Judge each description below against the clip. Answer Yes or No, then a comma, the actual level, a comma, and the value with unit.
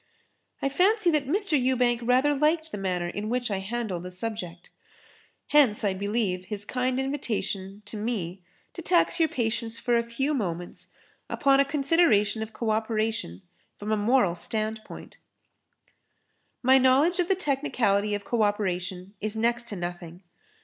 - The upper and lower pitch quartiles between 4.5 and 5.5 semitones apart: Yes, average, 5.0 semitones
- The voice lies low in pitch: No, high, 225 Hz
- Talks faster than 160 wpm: No, average, 155 wpm